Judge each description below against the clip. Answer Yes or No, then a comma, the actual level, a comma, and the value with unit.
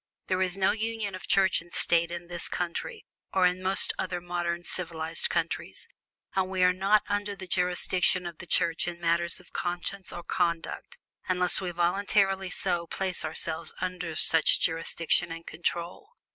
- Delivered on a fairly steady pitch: Yes, narrow, 1.8 semitones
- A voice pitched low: No, medium, 180 Hz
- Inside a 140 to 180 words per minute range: Yes, average, 165 wpm